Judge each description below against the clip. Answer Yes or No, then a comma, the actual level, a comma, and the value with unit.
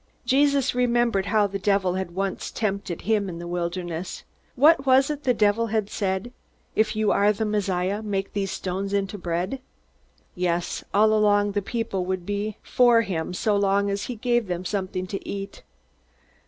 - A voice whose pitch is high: Yes, high, 200 Hz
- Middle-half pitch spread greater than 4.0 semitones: No, average, 2.7 semitones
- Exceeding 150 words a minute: Yes, average, 170 wpm